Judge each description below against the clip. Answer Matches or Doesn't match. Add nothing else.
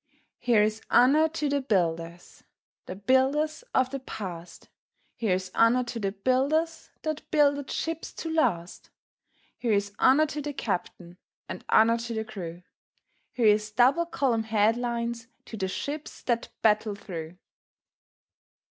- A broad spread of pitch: Matches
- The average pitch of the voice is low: Doesn't match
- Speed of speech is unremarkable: Doesn't match